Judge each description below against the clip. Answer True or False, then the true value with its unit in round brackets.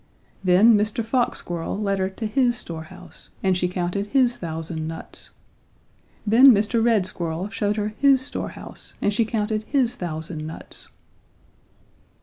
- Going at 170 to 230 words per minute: False (145 wpm)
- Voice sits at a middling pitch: False (205 Hz)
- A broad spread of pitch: False (4.5 semitones)